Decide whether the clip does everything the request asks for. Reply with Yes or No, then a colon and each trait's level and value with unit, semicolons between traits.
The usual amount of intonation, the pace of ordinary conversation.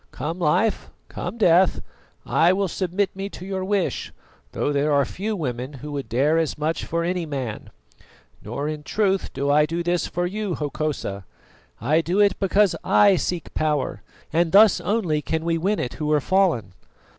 Yes: average, 4.2 semitones; average, 180 wpm